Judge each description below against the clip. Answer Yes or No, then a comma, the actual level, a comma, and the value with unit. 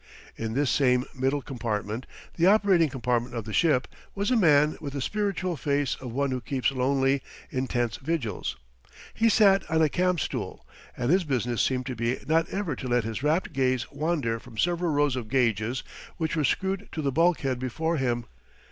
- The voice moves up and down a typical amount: Yes, average, 5.0 semitones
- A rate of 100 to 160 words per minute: No, average, 185 wpm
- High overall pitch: No, low, 135 Hz